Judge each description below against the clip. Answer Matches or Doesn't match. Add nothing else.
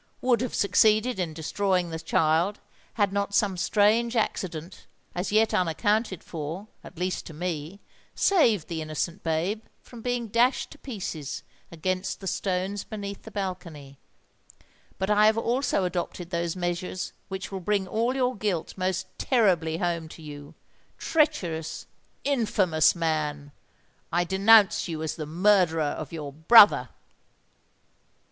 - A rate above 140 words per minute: Doesn't match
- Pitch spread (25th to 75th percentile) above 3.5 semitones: Matches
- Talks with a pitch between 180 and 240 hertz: Matches